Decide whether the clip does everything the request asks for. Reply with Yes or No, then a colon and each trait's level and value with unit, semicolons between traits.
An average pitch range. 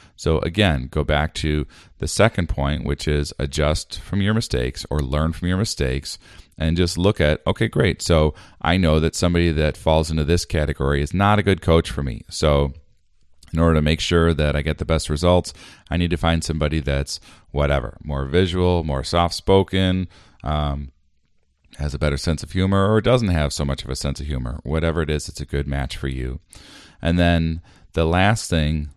Yes: average, 3.3 semitones